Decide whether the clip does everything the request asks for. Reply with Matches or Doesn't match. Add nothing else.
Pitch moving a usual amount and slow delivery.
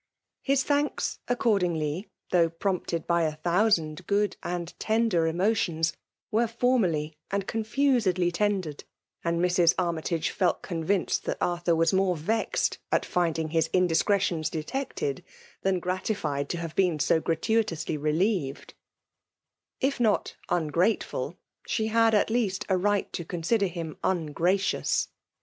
Matches